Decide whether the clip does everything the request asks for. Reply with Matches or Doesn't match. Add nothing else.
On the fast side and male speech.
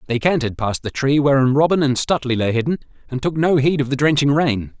Matches